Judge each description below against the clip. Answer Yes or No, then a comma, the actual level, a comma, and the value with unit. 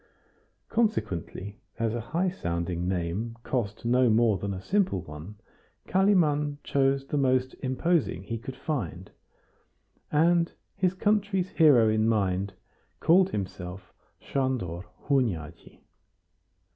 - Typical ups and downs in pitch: No, wide, 8.5 semitones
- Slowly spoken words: Yes, slow, 110 wpm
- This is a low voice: Yes, low, 120 Hz